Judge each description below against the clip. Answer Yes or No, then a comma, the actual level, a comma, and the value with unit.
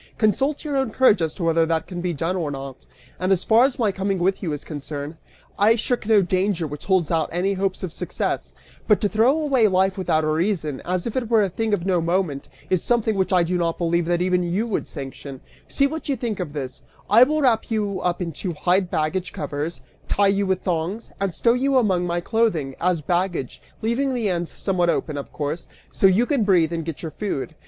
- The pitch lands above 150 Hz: Yes, medium, 185 Hz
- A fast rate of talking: Yes, fast, 230 wpm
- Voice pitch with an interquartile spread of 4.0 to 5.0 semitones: Yes, average, 4.5 semitones